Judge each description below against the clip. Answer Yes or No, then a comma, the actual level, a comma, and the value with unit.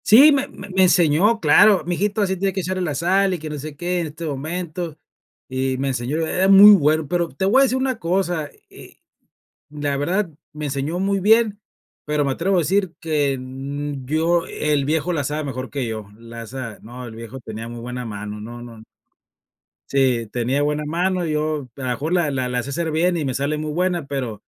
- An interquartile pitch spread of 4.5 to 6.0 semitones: Yes, average, 5.2 semitones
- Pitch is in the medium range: Yes, medium, 150 Hz